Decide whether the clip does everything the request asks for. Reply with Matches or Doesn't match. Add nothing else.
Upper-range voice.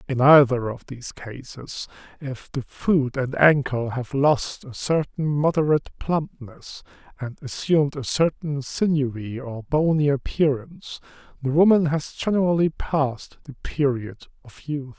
Doesn't match